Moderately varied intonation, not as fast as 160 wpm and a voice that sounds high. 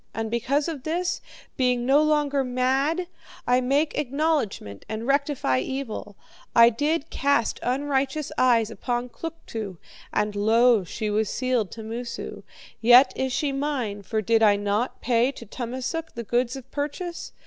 Yes: average, 4.1 semitones; average, 150 wpm; very high, 250 Hz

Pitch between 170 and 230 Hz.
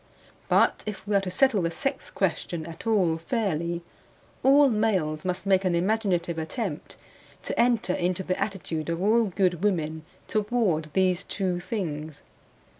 Yes: medium, 185 Hz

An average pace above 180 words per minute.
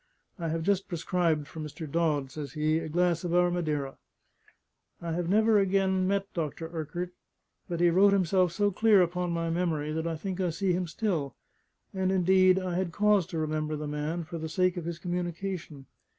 Yes: average, 195 wpm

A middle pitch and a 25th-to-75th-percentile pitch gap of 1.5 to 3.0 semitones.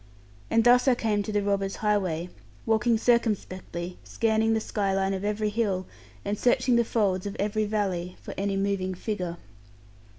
No: high, 205 Hz; narrow, 2.5 semitones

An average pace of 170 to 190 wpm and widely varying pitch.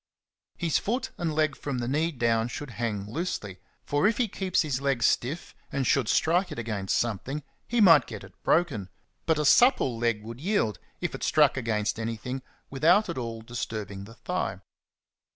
Yes: average, 180 wpm; wide, 6.4 semitones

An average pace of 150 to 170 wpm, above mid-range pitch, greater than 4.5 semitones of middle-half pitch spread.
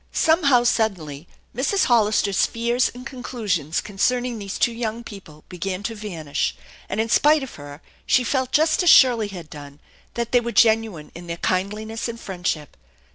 Yes: average, 165 wpm; high, 220 Hz; average, 5.2 semitones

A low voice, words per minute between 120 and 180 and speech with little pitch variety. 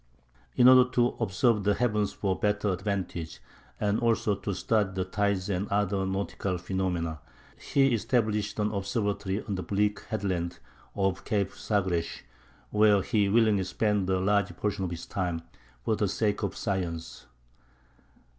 Yes: low, 100 Hz; average, 145 wpm; narrow, 2.1 semitones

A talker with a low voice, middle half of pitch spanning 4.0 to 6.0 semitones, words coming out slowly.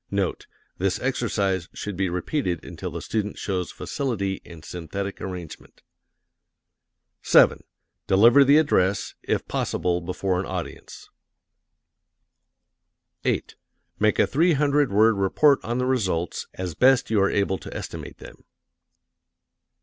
Yes: low, 100 Hz; average, 5.3 semitones; slow, 125 wpm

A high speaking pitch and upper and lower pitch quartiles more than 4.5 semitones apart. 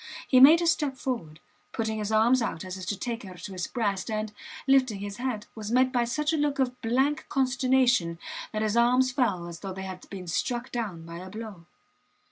Yes: high, 230 Hz; average, 5.1 semitones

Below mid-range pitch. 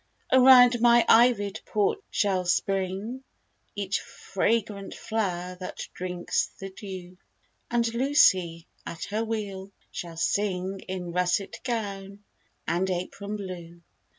No: high, 195 Hz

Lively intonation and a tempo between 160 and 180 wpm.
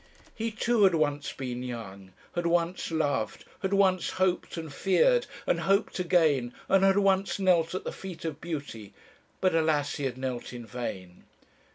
Yes: wide, 6.5 semitones; average, 170 wpm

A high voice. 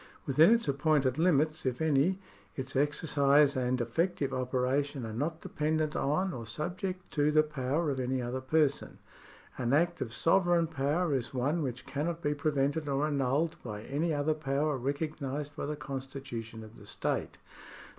No: medium, 145 Hz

